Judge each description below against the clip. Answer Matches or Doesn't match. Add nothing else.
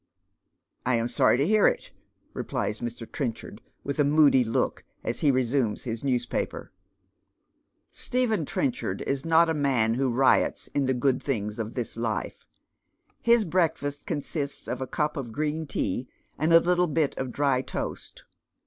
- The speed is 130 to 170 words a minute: Matches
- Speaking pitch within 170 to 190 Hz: Doesn't match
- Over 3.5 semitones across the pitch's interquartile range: Matches